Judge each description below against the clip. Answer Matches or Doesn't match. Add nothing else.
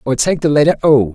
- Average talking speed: Doesn't match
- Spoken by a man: Matches